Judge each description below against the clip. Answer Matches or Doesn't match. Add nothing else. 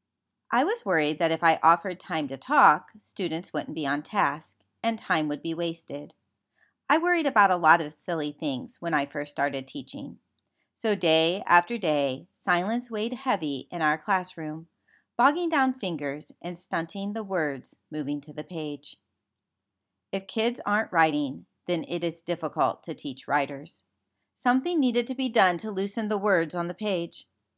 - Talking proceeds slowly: Doesn't match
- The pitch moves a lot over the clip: Matches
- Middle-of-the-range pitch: Matches